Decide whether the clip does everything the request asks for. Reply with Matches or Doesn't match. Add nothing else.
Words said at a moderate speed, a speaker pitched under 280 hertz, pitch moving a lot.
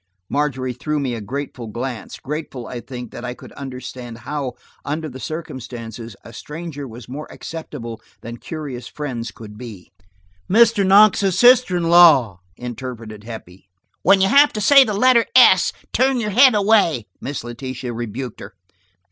Matches